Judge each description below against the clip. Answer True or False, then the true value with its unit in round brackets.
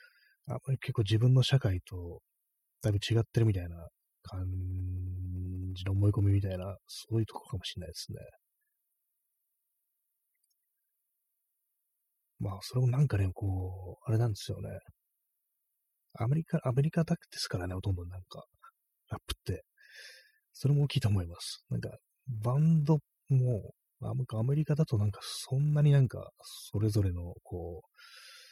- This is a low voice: True (110 Hz)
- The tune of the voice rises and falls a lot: True (6.5 semitones)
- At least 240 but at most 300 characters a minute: True (285 characters per minute)